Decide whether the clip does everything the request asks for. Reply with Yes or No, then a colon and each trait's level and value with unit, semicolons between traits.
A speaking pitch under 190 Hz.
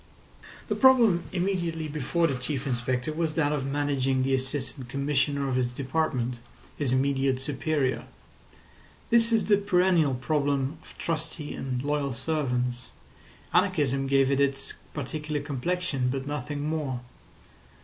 Yes: medium, 140 Hz